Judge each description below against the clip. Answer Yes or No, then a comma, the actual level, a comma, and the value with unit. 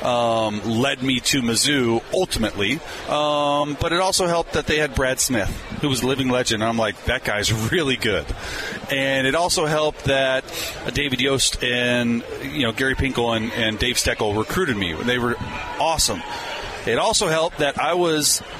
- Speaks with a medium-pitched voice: No, low, 130 Hz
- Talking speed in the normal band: Yes, average, 180 wpm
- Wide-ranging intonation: No, average, 4.0 semitones